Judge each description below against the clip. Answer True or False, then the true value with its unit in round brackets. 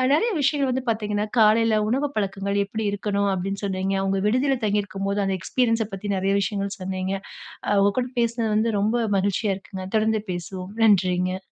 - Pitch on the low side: False (205 Hz)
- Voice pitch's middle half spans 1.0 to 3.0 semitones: True (2.4 semitones)